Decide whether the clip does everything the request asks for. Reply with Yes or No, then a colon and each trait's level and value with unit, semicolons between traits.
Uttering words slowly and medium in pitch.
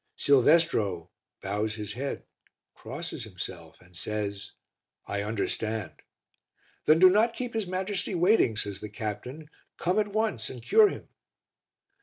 No: slow, 130 wpm; low, 125 Hz